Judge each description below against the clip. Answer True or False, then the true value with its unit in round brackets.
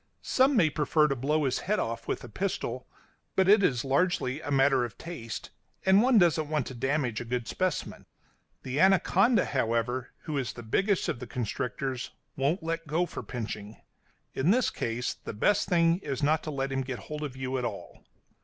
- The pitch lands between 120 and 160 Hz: True (140 Hz)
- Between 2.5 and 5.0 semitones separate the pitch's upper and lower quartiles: False (5.5 semitones)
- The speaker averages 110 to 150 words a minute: False (195 wpm)